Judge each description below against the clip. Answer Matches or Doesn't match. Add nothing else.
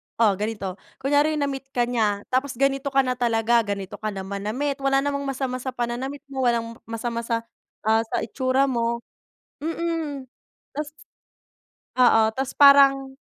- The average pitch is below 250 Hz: Doesn't match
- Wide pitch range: Doesn't match